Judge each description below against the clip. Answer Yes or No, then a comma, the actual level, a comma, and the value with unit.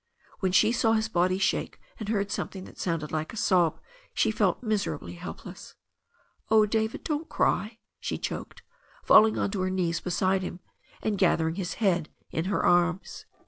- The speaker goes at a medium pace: Yes, average, 175 wpm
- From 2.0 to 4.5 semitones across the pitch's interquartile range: Yes, average, 3.6 semitones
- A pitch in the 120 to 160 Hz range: No, high, 190 Hz